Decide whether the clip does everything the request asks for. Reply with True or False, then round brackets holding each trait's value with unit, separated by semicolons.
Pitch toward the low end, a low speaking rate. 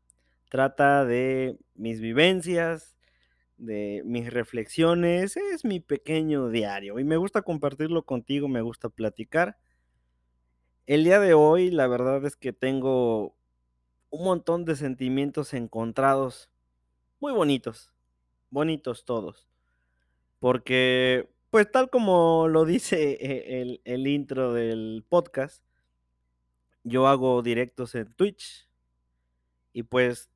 True (125 Hz; 110 wpm)